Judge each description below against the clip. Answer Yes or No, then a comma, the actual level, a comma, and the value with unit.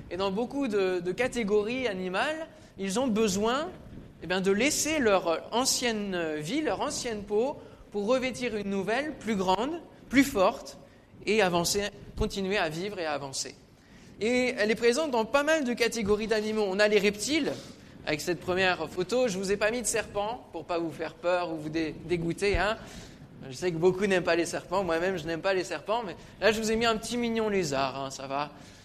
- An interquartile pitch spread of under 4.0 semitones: No, average, 5.0 semitones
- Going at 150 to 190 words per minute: No, average, 210 wpm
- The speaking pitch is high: Yes, high, 200 Hz